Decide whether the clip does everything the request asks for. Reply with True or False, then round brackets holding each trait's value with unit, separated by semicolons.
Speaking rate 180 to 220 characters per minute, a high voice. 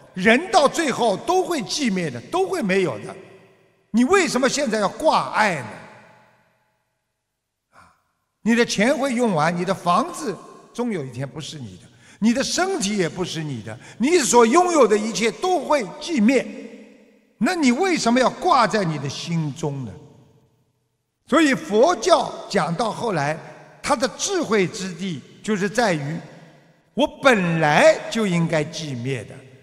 True (210 characters per minute; 215 Hz)